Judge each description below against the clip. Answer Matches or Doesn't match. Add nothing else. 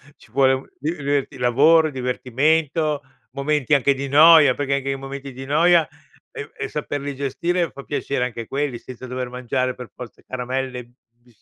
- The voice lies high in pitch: Doesn't match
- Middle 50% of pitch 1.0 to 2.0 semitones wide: Doesn't match